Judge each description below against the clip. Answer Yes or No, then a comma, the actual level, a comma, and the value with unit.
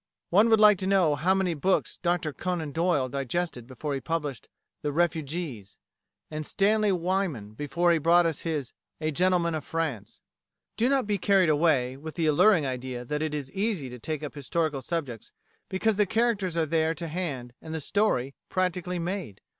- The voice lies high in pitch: No, medium, 165 Hz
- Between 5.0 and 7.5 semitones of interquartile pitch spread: No, average, 4.5 semitones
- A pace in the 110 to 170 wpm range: No, average, 180 wpm